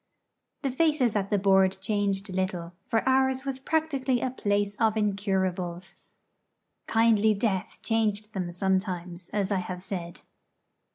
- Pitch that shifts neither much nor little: Yes, average, 3.3 semitones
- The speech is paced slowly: Yes, slow, 130 wpm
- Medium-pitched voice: No, high, 205 Hz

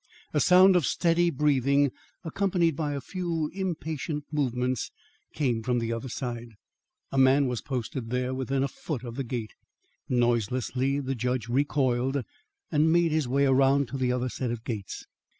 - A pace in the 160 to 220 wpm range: Yes, average, 165 wpm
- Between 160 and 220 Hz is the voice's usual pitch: No, low, 135 Hz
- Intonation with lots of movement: No, average, 3.3 semitones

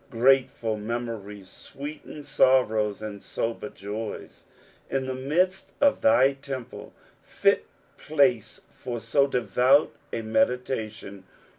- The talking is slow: Yes, slow, 100 wpm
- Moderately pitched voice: No, low, 125 Hz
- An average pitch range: Yes, average, 4.0 semitones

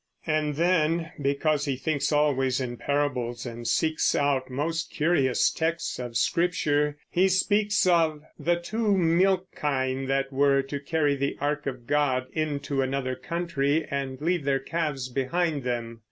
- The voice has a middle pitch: Yes, medium, 145 Hz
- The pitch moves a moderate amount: Yes, average, 3.5 semitones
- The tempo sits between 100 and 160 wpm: Yes, average, 150 wpm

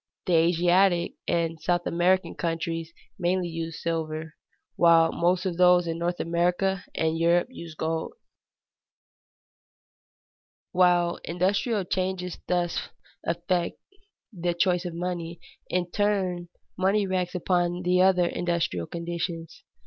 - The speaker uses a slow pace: Yes, slow, 115 wpm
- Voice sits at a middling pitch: Yes, medium, 175 Hz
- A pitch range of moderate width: No, narrow, 1.4 semitones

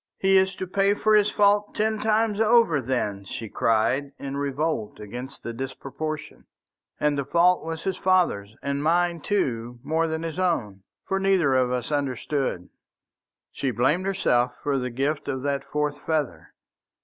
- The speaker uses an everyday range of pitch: No, wide, 6.5 semitones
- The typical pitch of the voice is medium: Yes, medium, 150 Hz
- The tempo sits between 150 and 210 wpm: Yes, average, 160 wpm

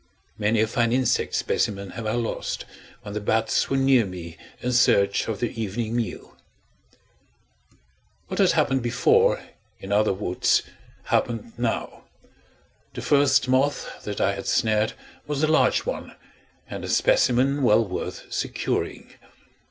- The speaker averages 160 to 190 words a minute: No, average, 140 wpm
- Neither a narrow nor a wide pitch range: Yes, average, 3.6 semitones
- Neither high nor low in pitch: No, low, 115 Hz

